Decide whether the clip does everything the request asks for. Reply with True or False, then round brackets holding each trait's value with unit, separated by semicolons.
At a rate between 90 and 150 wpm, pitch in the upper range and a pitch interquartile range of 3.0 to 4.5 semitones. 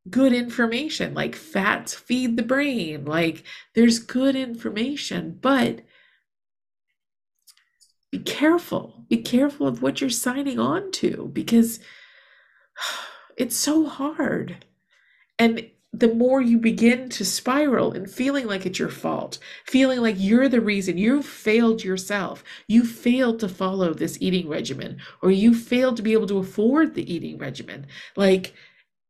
False (135 wpm; 230 Hz; 5.1 semitones)